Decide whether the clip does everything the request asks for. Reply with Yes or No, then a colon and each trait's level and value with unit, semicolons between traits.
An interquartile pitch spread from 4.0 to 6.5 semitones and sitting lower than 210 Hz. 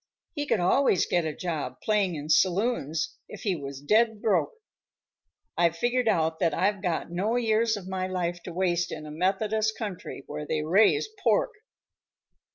Yes: average, 4.9 semitones; medium, 185 Hz